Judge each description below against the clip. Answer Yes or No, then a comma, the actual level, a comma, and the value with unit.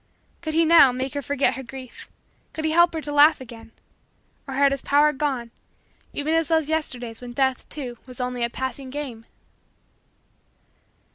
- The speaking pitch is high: Yes, very high, 270 Hz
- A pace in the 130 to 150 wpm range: No, average, 170 wpm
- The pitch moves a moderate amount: Yes, average, 3.3 semitones